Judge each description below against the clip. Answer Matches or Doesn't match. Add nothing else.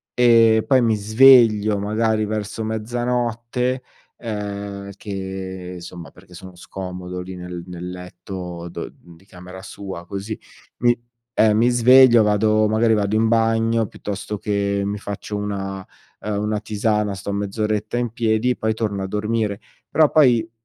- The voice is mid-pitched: Doesn't match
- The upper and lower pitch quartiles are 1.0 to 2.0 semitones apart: Doesn't match